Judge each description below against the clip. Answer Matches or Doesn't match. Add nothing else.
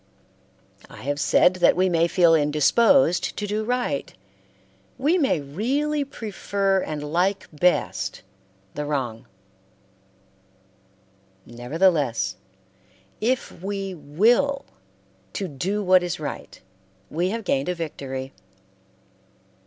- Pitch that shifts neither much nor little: Doesn't match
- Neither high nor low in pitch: Matches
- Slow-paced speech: Matches